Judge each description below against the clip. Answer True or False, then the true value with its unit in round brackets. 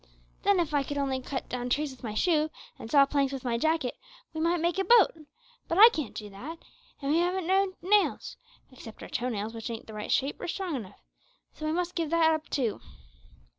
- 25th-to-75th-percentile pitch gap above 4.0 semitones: True (5.4 semitones)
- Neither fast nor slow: False (225 wpm)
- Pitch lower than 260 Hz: False (295 Hz)